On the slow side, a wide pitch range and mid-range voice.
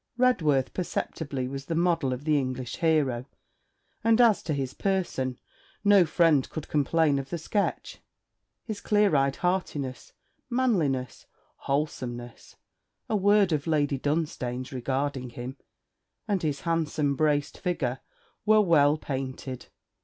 No: slow, 125 wpm; average, 4.9 semitones; medium, 150 Hz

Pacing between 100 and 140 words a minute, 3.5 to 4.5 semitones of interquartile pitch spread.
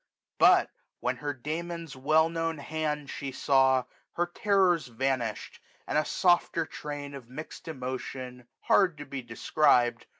Yes: slow, 135 wpm; average, 3.8 semitones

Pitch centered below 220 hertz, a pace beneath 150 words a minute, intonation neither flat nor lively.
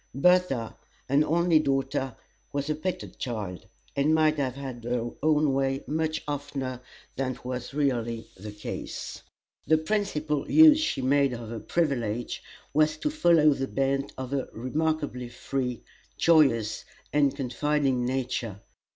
Yes: low, 135 Hz; slow, 135 wpm; average, 3.6 semitones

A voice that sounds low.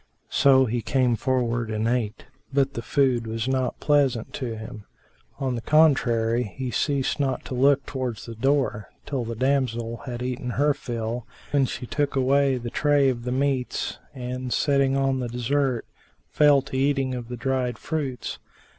Yes: low, 130 Hz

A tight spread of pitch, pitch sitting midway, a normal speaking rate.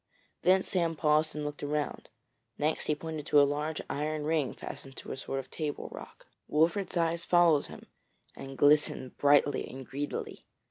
Yes: narrow, 2.0 semitones; medium, 150 Hz; average, 170 wpm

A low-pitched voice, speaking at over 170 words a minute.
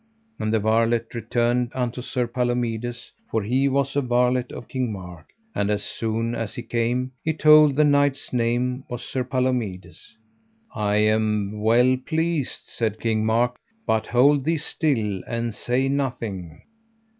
No: low, 120 Hz; average, 150 wpm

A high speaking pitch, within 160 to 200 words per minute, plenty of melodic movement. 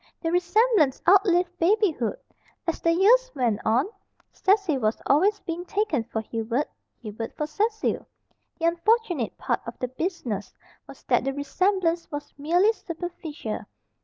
No: very high, 335 Hz; slow, 135 wpm; wide, 6.7 semitones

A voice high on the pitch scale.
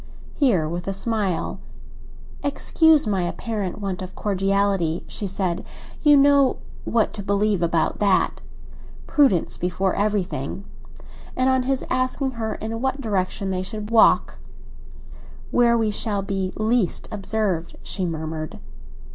Yes: high, 200 Hz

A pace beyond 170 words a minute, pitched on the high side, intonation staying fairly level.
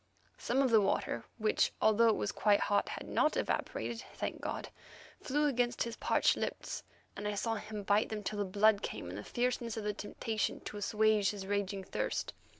Yes: average, 195 wpm; high, 215 Hz; narrow, 2.3 semitones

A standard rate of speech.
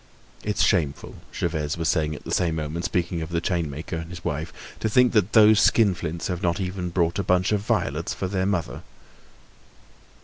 Yes: average, 190 wpm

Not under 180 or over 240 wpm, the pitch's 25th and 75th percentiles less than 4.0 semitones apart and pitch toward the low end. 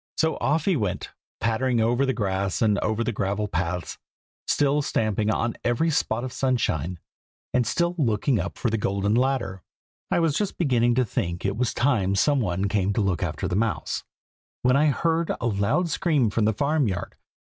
No: average, 190 wpm; wide, 5.5 semitones; low, 115 Hz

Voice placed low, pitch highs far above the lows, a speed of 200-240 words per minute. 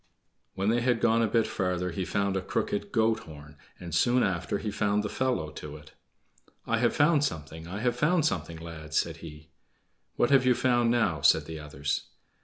Yes: low, 100 Hz; wide, 6.7 semitones; fast, 205 wpm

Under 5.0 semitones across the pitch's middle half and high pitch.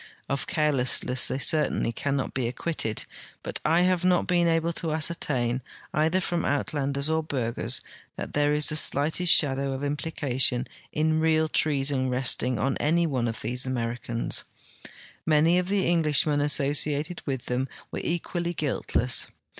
No: average, 3.6 semitones; medium, 145 Hz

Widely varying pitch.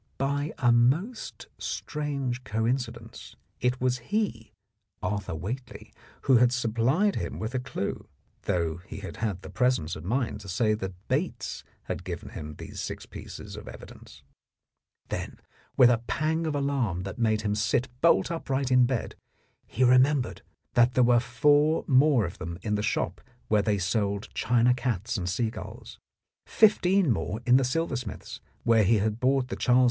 No: average, 4.2 semitones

